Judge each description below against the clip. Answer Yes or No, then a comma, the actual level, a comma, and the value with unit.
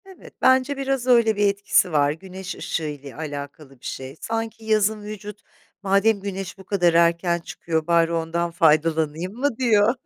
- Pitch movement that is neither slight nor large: Yes, average, 5.0 semitones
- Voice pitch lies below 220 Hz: Yes, high, 190 Hz